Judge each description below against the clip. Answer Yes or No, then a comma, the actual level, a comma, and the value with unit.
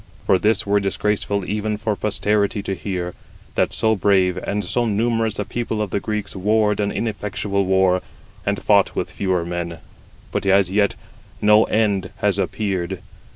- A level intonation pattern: Yes, narrow, 1.9 semitones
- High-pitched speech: No, low, 100 Hz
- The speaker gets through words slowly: No, average, 160 wpm